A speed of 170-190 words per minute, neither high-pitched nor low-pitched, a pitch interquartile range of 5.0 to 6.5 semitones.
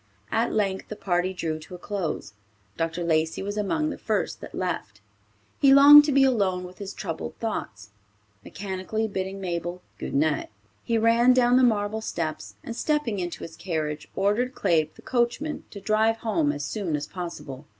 No: average, 175 wpm; high, 195 Hz; wide, 5.4 semitones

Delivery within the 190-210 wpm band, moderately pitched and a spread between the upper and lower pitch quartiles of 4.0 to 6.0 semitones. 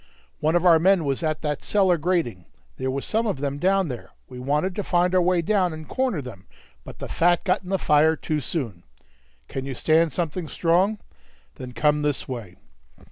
Yes: average, 200 wpm; medium, 160 Hz; average, 4.6 semitones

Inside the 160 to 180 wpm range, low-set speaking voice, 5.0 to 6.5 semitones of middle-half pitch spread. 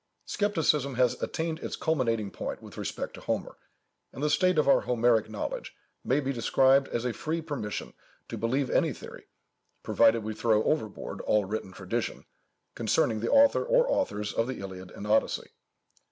Yes: average, 170 wpm; low, 120 Hz; wide, 5.6 semitones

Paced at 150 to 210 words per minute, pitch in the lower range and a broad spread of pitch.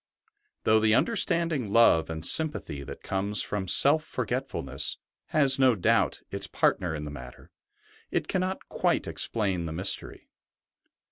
No: average, 140 wpm; low, 110 Hz; wide, 8.6 semitones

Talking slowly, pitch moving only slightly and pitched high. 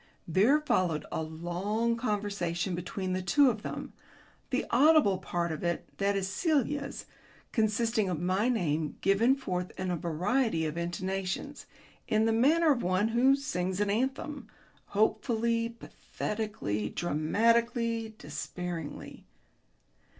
No: slow, 125 wpm; average, 4.8 semitones; high, 205 Hz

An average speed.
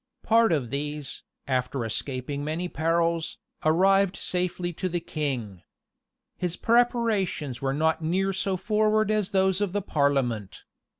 No: slow, 130 wpm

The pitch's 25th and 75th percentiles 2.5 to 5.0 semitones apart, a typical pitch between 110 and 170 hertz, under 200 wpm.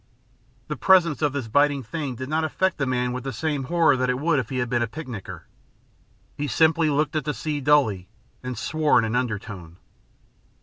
No: average, 3.8 semitones; low, 135 Hz; fast, 205 wpm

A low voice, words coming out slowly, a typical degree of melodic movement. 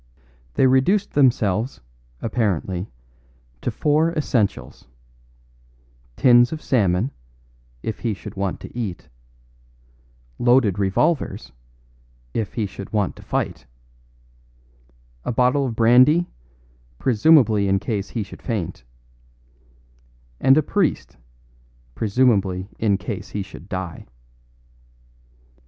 Yes: low, 110 Hz; slow, 100 wpm; average, 5.0 semitones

